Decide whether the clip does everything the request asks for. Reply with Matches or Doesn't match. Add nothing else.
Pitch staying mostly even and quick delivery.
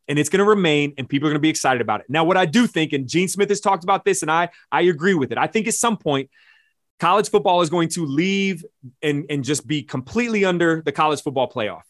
Doesn't match